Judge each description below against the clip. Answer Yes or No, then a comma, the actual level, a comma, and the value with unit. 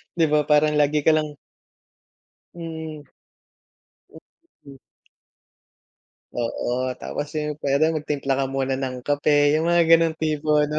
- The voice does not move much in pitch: Yes, narrow, 1.8 semitones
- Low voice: No, medium, 150 Hz